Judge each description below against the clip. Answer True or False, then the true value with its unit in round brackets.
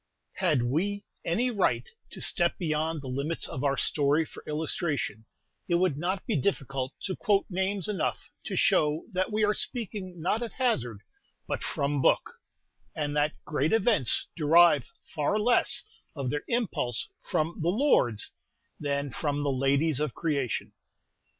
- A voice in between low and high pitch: True (155 Hz)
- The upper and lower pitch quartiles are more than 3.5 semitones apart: True (5.1 semitones)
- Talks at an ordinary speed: True (150 wpm)